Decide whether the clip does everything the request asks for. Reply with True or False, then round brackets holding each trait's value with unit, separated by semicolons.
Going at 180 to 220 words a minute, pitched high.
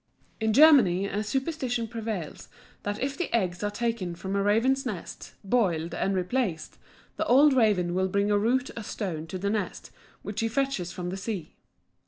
True (185 wpm; 210 Hz)